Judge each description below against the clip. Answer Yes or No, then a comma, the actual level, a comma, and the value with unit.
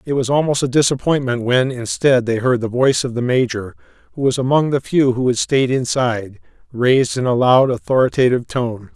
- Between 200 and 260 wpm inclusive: No, average, 180 wpm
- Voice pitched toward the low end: Yes, low, 125 Hz